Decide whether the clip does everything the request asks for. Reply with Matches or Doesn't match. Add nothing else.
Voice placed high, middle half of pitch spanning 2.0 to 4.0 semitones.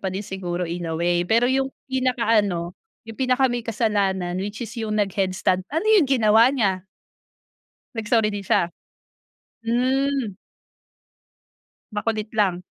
Doesn't match